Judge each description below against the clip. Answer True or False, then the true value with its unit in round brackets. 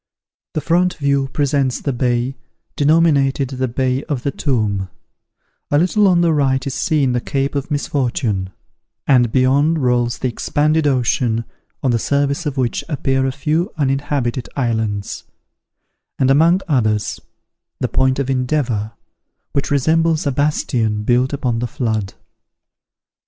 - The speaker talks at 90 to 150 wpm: True (140 wpm)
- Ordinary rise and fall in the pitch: True (3.1 semitones)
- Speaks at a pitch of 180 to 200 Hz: False (135 Hz)